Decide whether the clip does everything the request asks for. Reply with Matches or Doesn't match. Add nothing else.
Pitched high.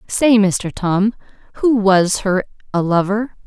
Matches